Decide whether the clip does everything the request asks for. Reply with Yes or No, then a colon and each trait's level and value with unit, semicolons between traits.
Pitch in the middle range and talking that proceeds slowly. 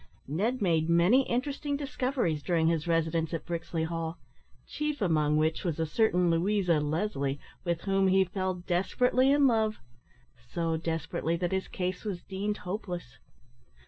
No: medium, 175 Hz; average, 145 wpm